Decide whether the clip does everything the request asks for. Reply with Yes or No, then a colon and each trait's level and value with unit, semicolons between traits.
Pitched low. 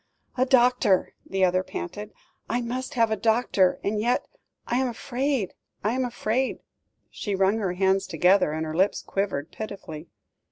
No: high, 210 Hz